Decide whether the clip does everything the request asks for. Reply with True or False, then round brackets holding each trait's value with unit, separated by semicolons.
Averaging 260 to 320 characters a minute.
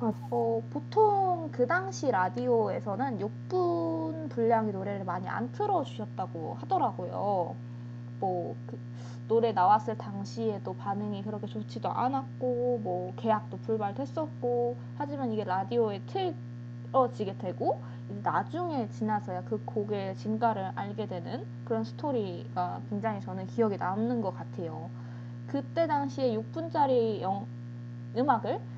True (270 characters per minute)